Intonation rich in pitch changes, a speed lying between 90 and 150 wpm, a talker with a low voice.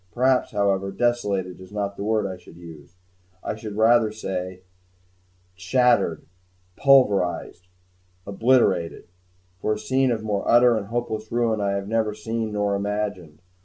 No: average, 3.0 semitones; average, 140 wpm; low, 105 Hz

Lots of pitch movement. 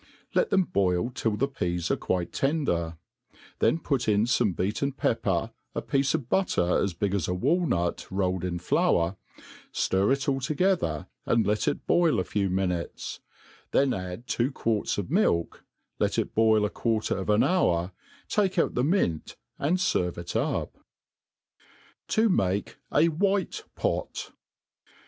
Yes: wide, 7.9 semitones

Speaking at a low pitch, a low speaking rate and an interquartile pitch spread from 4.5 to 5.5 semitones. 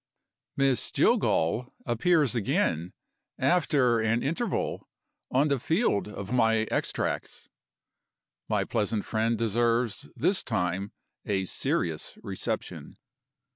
Yes: low, 115 Hz; slow, 95 wpm; average, 4.8 semitones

